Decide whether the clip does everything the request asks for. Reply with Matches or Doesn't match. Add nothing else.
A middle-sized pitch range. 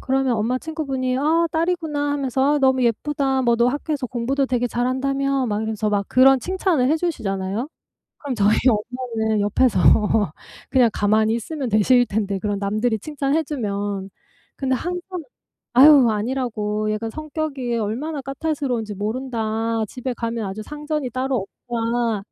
Matches